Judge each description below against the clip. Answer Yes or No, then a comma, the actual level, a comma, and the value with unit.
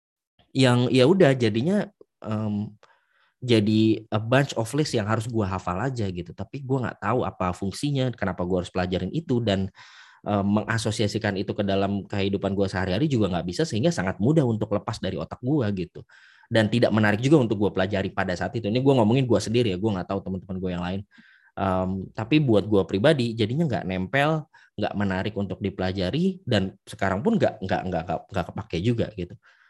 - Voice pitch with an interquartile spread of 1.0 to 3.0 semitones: No, average, 4.3 semitones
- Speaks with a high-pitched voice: No, low, 105 Hz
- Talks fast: Yes, fast, 190 wpm